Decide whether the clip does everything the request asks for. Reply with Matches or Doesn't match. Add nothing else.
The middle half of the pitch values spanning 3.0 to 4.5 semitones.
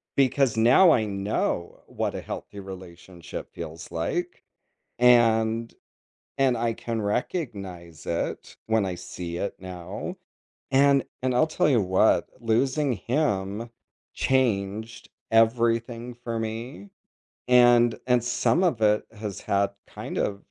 Matches